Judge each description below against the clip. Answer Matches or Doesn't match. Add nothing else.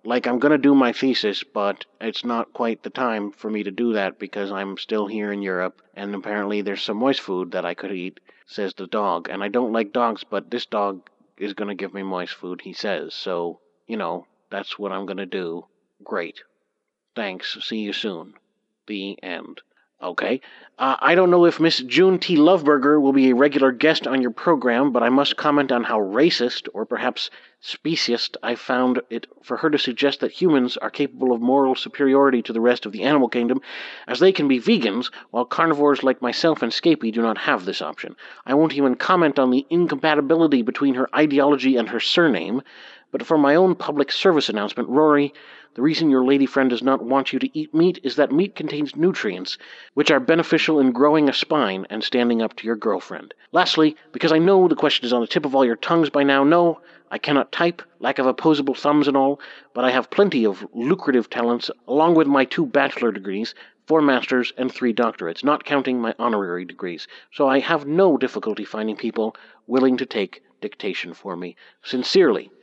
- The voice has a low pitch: Matches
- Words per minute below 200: Doesn't match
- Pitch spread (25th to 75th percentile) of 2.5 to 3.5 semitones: Doesn't match